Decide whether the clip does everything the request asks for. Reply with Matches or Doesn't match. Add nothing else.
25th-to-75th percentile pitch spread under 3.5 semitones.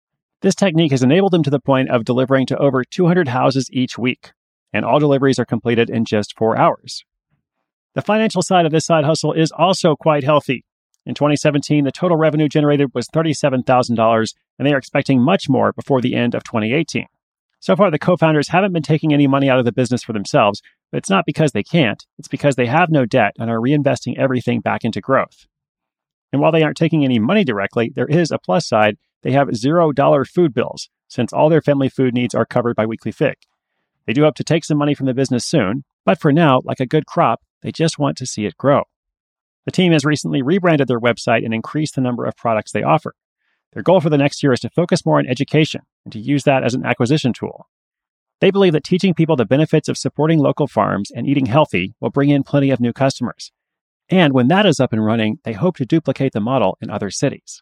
Doesn't match